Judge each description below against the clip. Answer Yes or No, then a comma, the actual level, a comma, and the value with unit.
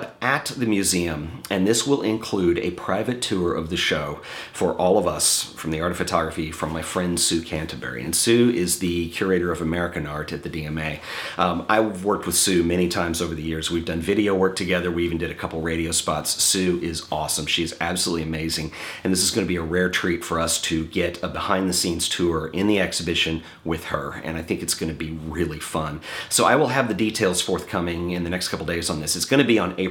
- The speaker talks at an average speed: No, fast, 235 wpm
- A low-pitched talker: Yes, very low, 85 Hz